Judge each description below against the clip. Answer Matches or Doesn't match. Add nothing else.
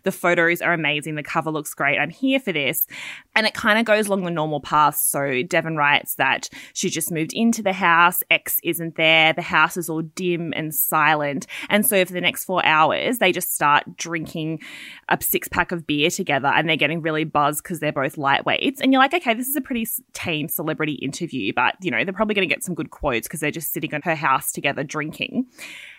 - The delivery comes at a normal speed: Doesn't match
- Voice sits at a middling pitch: Matches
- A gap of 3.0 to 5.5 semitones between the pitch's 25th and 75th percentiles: Matches